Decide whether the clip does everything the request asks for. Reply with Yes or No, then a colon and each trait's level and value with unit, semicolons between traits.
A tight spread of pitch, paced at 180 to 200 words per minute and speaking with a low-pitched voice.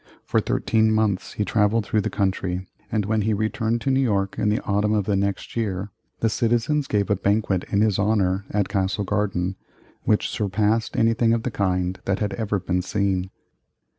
Yes: narrow, 2.2 semitones; average, 190 wpm; low, 105 Hz